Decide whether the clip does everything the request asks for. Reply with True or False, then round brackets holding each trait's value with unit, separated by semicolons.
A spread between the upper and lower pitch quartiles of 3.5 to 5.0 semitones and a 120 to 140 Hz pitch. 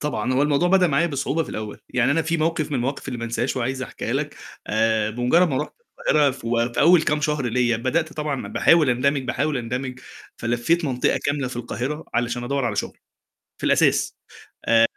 True (3.8 semitones; 135 Hz)